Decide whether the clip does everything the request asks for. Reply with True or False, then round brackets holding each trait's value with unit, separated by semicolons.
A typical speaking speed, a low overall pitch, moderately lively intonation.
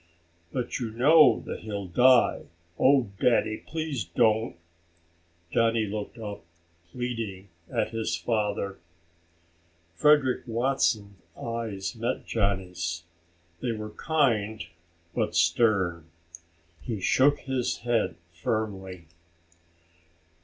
False (95 wpm; 110 Hz; 3.6 semitones)